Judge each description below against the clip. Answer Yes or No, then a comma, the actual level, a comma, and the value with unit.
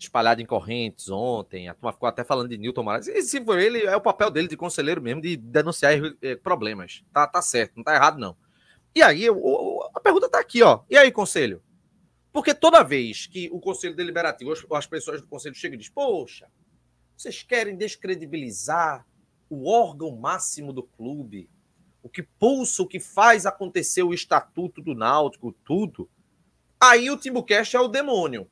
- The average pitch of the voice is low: No, medium, 175 Hz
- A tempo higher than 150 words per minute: Yes, average, 180 wpm